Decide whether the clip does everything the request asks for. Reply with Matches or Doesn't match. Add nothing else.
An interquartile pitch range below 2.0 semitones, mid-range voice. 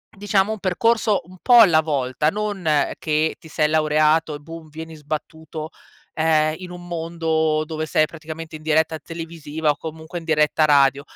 Matches